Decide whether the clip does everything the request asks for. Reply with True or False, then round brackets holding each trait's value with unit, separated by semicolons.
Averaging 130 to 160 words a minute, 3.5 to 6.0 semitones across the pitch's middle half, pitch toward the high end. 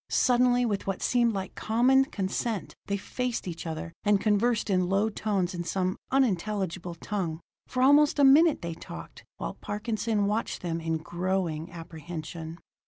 True (155 wpm; 5.2 semitones; 195 Hz)